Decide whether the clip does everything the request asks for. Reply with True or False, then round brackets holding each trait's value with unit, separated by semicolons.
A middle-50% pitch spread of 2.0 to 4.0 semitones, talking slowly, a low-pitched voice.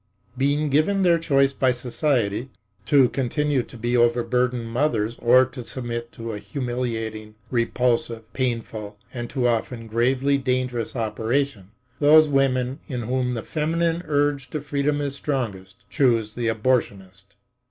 True (3.4 semitones; 130 wpm; 125 Hz)